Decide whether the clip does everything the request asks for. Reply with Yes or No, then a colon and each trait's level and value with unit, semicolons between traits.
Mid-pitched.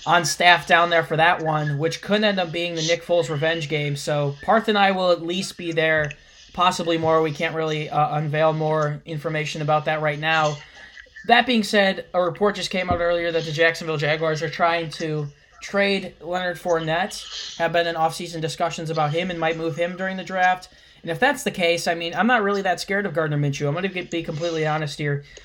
Yes: medium, 165 Hz